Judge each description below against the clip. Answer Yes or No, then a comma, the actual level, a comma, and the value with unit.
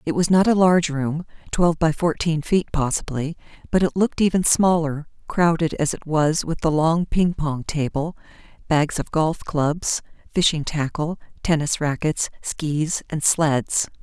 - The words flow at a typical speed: Yes, average, 150 wpm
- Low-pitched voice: No, medium, 160 Hz